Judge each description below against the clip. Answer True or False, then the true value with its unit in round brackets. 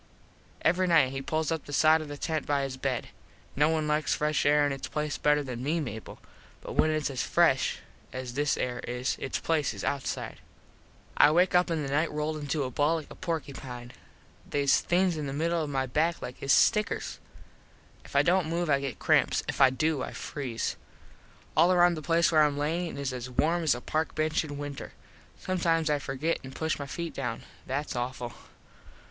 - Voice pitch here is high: False (150 Hz)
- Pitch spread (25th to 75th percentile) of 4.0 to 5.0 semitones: False (3.0 semitones)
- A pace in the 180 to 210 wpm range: True (205 wpm)